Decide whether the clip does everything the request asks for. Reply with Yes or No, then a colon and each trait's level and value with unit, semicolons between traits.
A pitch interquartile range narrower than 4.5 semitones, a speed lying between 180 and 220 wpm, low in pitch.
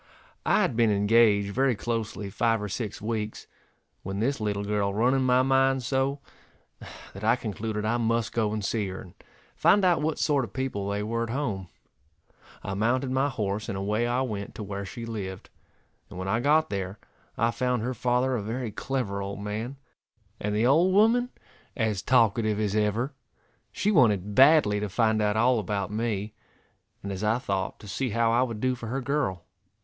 Yes: average, 3.8 semitones; average, 190 wpm; low, 110 Hz